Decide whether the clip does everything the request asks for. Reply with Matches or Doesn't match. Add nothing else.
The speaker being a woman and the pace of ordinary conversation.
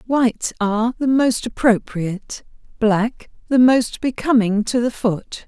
Doesn't match